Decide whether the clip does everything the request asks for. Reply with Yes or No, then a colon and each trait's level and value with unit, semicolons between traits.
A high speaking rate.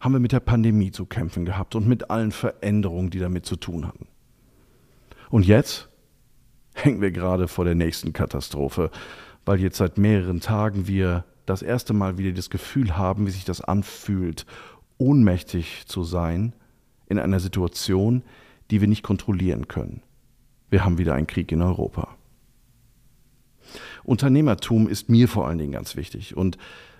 No: average, 155 wpm